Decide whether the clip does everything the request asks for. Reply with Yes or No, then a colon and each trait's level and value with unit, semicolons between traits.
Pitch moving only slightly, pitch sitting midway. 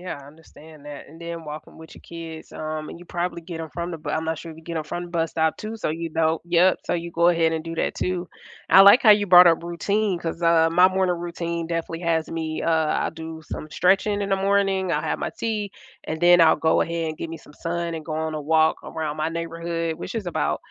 Yes: narrow, 1.7 semitones; medium, 165 Hz